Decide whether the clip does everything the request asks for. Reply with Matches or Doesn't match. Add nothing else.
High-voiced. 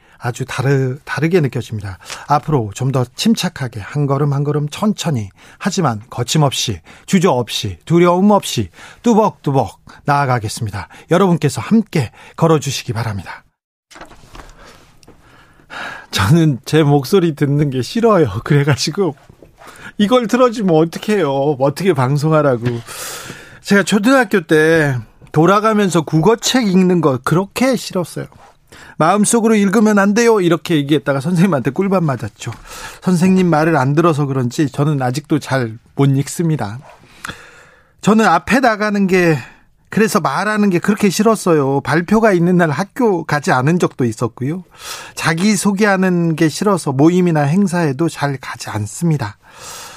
Doesn't match